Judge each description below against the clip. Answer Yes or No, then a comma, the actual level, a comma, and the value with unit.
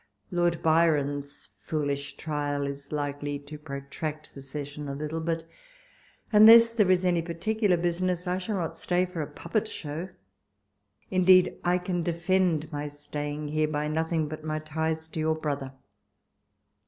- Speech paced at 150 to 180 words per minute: Yes, average, 155 wpm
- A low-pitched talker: No, medium, 160 Hz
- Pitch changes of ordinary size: Yes, average, 3.2 semitones